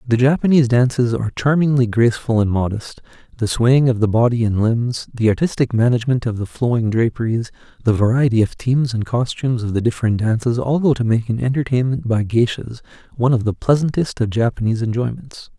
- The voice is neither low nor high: No, low, 120 Hz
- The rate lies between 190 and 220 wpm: No, average, 180 wpm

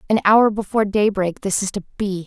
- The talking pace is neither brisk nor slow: No, fast, 210 wpm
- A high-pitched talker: Yes, high, 200 Hz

